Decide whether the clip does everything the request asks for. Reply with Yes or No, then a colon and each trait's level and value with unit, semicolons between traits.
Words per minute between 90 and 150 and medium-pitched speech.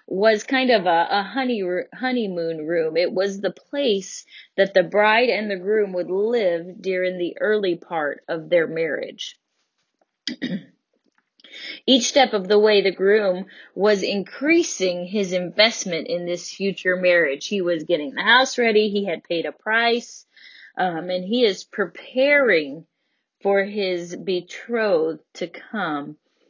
No: average, 145 wpm; high, 195 Hz